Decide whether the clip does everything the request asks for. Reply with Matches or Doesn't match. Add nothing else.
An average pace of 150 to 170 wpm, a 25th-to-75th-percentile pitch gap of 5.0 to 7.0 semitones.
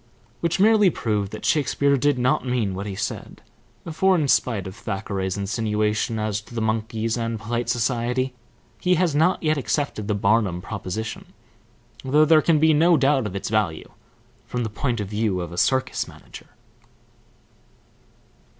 Matches